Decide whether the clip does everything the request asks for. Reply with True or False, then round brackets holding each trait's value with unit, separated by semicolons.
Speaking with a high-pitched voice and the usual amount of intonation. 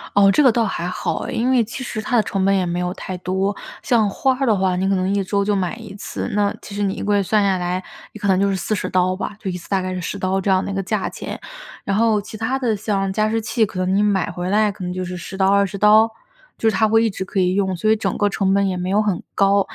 False (200 Hz; 2.3 semitones)